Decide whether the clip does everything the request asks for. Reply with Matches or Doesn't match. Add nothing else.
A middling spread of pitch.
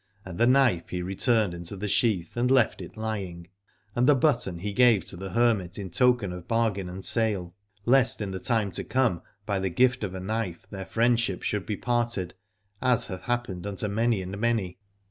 Matches